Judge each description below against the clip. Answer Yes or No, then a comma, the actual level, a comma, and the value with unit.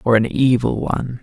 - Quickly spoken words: No, average, 195 wpm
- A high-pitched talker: No, low, 120 Hz